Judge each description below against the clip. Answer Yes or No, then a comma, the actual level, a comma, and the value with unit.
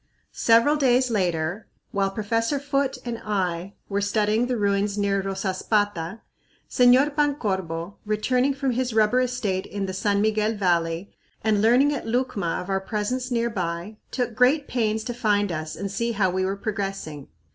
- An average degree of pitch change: Yes, average, 4.0 semitones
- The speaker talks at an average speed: Yes, average, 160 wpm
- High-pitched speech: Yes, high, 210 Hz